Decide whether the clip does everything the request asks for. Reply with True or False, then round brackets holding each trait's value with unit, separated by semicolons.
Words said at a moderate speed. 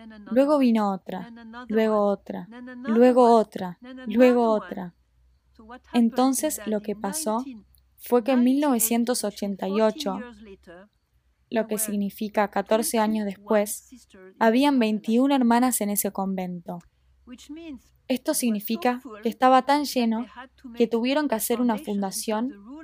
False (115 wpm)